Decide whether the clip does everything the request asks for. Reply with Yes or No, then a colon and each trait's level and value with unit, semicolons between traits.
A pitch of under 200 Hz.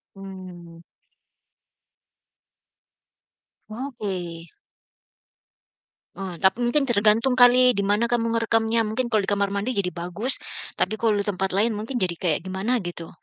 No: high, 205 Hz